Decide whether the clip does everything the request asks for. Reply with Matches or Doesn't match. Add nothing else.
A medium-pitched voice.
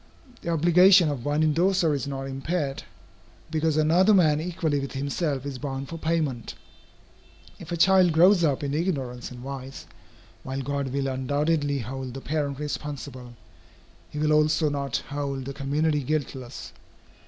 Matches